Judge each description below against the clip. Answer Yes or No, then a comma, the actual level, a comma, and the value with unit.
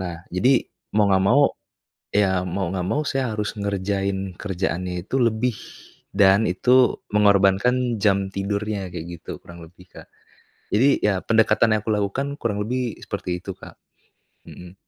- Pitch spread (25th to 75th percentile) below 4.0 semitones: Yes, average, 2.9 semitones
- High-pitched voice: No, low, 100 Hz